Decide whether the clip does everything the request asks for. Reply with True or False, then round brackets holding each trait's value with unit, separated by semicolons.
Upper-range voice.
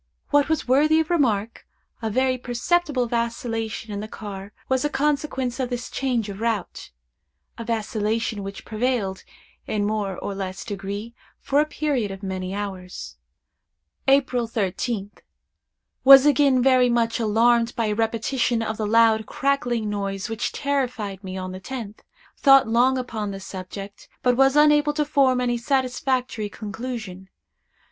True (230 Hz)